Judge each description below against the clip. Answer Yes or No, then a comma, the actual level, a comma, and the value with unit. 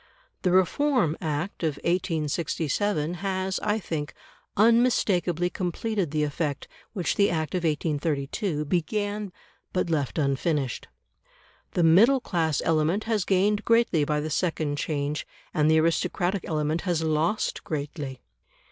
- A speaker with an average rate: No, slow, 125 wpm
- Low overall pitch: No, medium, 165 Hz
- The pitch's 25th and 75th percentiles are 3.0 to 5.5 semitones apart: Yes, average, 4.2 semitones